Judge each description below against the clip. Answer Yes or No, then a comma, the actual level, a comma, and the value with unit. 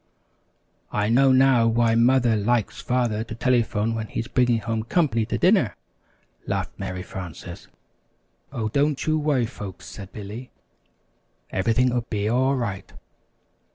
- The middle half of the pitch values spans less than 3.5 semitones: Yes, average, 2.9 semitones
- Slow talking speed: Yes, slow, 130 wpm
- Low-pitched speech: Yes, low, 115 Hz